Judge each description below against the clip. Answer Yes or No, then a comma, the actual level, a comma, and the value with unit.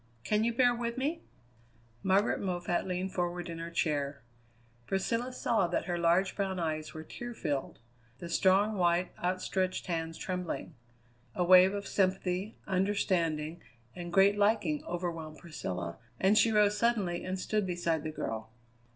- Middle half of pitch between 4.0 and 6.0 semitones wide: No, average, 3.2 semitones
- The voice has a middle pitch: Yes, medium, 180 Hz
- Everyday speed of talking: Yes, average, 150 wpm